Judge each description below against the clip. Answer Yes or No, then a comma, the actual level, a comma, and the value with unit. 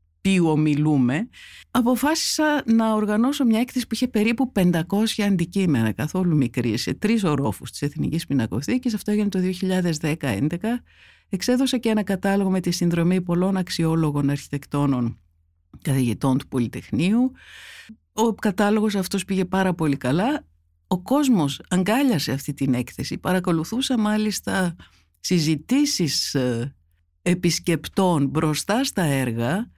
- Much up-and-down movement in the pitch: Yes, wide, 7.5 semitones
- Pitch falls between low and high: Yes, medium, 180 Hz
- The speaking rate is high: No, slow, 115 wpm